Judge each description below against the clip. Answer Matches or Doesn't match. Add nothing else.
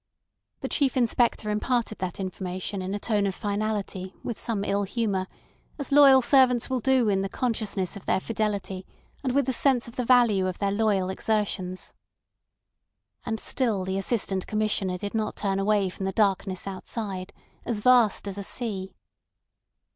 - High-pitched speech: Matches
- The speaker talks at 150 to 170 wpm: Matches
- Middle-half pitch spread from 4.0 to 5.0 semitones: Doesn't match